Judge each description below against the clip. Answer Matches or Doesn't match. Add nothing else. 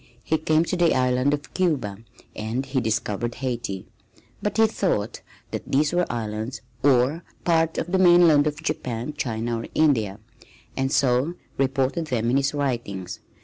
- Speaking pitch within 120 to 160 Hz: Matches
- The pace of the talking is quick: Doesn't match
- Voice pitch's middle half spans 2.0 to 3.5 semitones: Doesn't match